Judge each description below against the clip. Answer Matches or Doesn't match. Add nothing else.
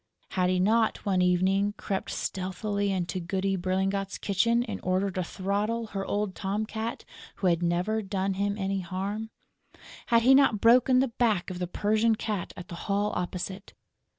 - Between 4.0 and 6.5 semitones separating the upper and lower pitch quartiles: Doesn't match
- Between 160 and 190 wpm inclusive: Matches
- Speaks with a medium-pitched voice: Doesn't match